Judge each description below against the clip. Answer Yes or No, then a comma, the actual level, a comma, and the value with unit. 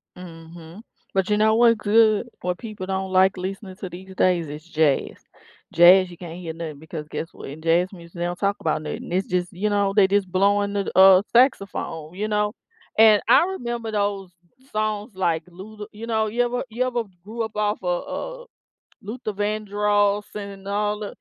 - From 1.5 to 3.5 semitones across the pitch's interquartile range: Yes, average, 3.1 semitones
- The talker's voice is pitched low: No, high, 200 Hz